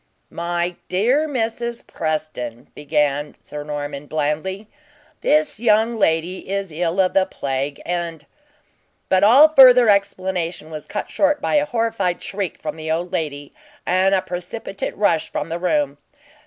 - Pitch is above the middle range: No, medium, 180 Hz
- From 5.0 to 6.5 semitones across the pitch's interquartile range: Yes, wide, 5.6 semitones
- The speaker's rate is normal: Yes, average, 145 wpm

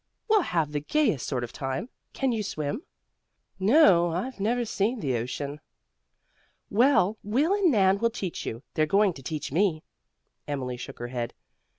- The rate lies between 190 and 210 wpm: No, average, 170 wpm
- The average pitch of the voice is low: No, medium, 185 Hz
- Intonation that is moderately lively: No, wide, 8.4 semitones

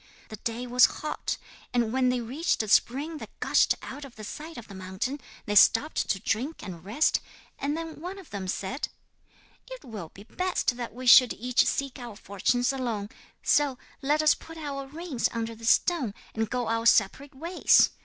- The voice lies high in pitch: Yes, very high, 250 Hz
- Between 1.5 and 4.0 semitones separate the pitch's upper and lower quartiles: No, average, 4.8 semitones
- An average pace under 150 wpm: No, average, 190 wpm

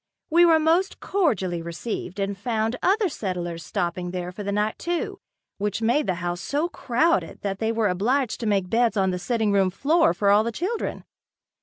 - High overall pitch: Yes, high, 215 Hz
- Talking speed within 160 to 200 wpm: Yes, average, 190 wpm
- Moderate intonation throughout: No, wide, 7.4 semitones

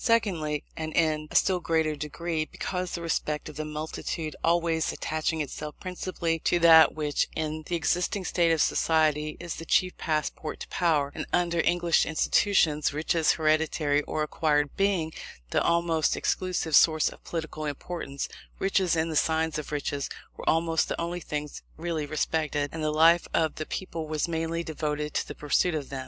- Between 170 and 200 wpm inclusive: Yes, average, 175 wpm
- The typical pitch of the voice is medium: Yes, medium, 160 Hz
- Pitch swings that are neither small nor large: No, narrow, 1.9 semitones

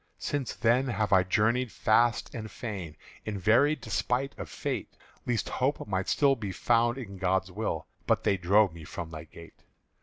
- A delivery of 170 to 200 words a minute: Yes, average, 175 wpm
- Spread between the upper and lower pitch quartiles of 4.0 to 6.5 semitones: Yes, average, 4.4 semitones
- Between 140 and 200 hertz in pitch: No, low, 110 Hz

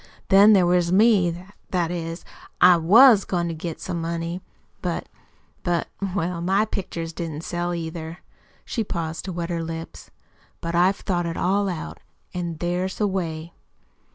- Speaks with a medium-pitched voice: Yes, medium, 175 Hz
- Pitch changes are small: Yes, narrow, 2.0 semitones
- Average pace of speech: Yes, average, 155 wpm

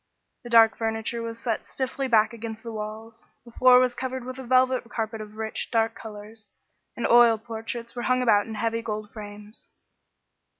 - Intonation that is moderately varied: No, narrow, 1.7 semitones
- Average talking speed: Yes, average, 180 wpm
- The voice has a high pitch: Yes, high, 230 Hz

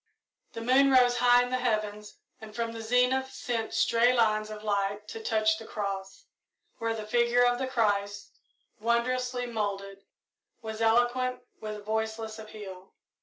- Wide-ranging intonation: No, narrow, 2.4 semitones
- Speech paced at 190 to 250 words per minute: No, average, 150 wpm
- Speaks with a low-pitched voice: No, high, 225 Hz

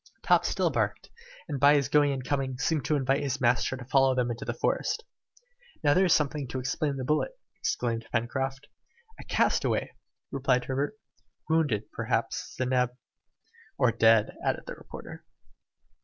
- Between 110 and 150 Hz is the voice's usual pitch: Yes, low, 135 Hz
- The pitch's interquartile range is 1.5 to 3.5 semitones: Yes, narrow, 2.5 semitones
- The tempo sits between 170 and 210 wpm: No, average, 155 wpm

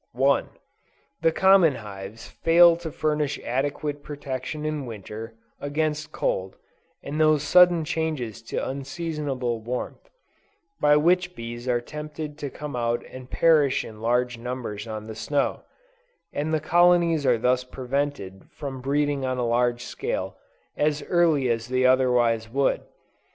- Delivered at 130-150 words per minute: Yes, average, 140 wpm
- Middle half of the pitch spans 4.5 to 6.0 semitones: No, average, 4.1 semitones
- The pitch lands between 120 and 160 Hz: Yes, low, 135 Hz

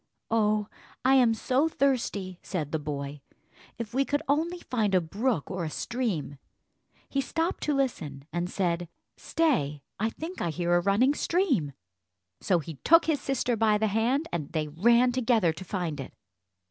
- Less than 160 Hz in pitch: No, high, 215 Hz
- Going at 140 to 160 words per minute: No, average, 170 wpm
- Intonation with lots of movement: Yes, wide, 7.6 semitones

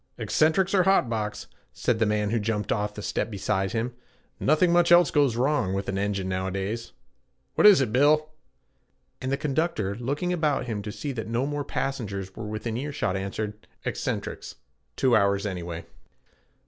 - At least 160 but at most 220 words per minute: Yes, average, 170 wpm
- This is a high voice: No, low, 115 Hz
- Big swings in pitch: Yes, wide, 6.1 semitones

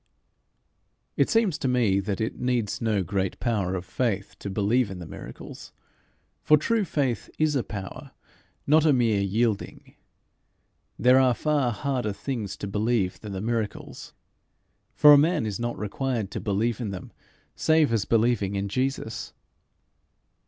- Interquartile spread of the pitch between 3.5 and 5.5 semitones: Yes, average, 4.7 semitones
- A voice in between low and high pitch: No, low, 115 Hz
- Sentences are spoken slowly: No, average, 150 wpm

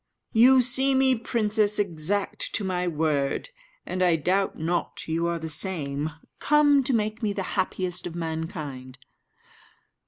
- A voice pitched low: No, medium, 185 Hz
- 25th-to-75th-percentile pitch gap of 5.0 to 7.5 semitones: Yes, average, 5.3 semitones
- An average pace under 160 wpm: Yes, average, 145 wpm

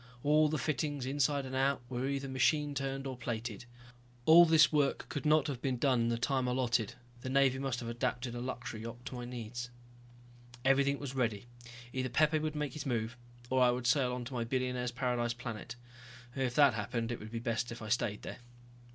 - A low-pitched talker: Yes, low, 125 Hz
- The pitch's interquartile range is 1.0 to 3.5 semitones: Yes, narrow, 2.4 semitones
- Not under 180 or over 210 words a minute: Yes, fast, 205 wpm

